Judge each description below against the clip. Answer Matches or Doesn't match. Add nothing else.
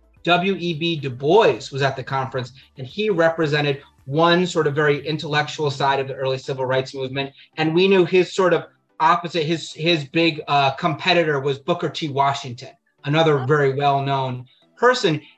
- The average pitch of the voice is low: Doesn't match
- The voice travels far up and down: Doesn't match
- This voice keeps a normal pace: Matches